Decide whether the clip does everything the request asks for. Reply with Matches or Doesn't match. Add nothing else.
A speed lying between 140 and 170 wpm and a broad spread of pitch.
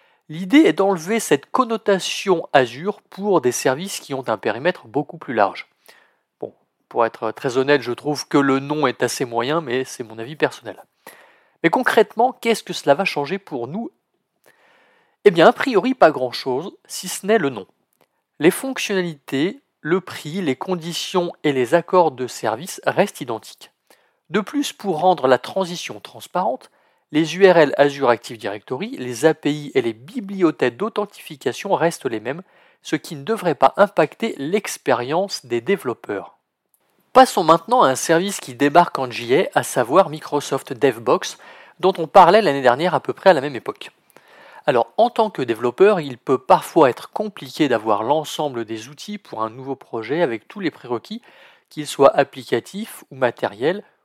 Matches